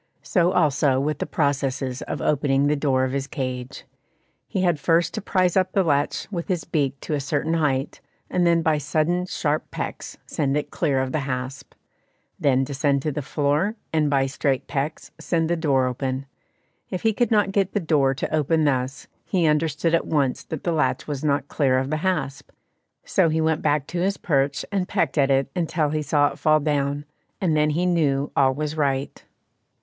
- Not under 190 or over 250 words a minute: Yes, average, 200 wpm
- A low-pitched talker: No, medium, 150 Hz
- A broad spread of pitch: No, average, 3.1 semitones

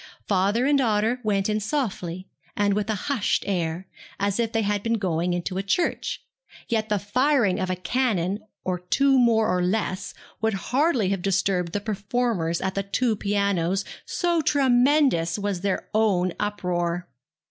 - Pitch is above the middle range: Yes, high, 205 Hz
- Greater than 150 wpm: Yes, average, 160 wpm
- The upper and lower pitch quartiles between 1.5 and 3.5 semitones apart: No, average, 3.9 semitones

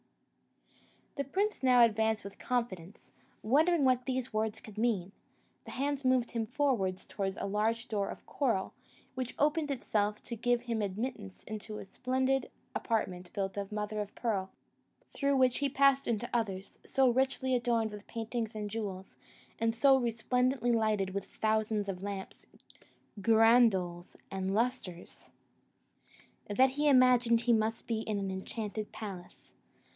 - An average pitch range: Yes, average, 3.8 semitones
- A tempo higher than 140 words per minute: Yes, average, 150 wpm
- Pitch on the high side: Yes, high, 225 Hz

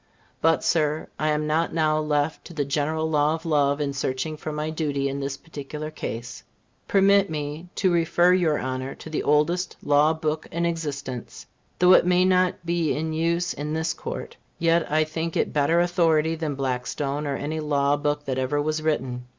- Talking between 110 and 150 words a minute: No, average, 190 wpm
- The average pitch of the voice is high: No, medium, 155 Hz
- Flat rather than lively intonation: Yes, narrow, 2.3 semitones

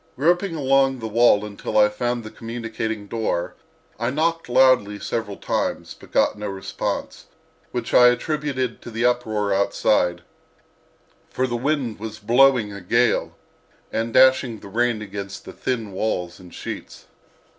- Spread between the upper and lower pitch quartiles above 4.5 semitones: No, average, 3.7 semitones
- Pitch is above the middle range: No, low, 115 Hz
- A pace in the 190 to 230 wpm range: No, average, 145 wpm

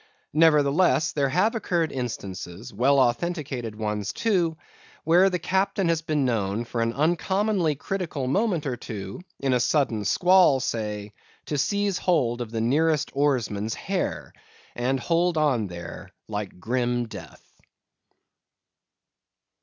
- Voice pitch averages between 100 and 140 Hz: Yes, low, 135 Hz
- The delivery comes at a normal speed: No, slow, 125 wpm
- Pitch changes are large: Yes, wide, 6.6 semitones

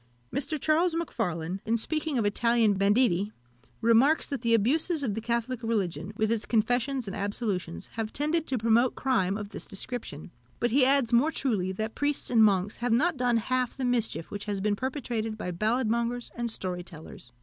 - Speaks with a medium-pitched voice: No, high, 230 Hz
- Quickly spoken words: No, average, 185 wpm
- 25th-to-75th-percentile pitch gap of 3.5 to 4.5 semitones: Yes, average, 3.9 semitones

